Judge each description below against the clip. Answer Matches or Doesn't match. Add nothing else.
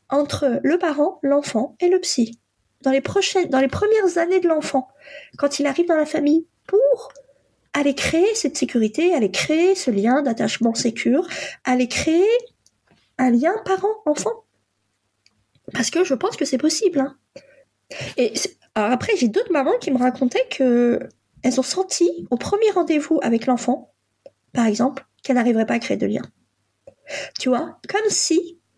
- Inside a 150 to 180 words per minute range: Matches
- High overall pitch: Matches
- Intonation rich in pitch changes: Matches